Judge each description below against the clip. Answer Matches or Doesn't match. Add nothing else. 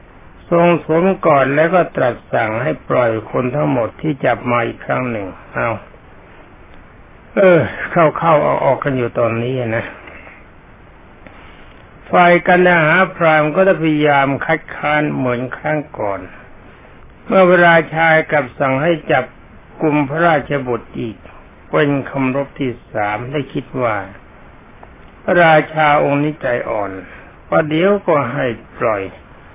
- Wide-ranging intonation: Doesn't match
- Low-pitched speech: Doesn't match